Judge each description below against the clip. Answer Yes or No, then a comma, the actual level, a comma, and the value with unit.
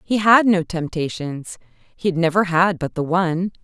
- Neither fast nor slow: Yes, average, 180 wpm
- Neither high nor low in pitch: Yes, medium, 175 Hz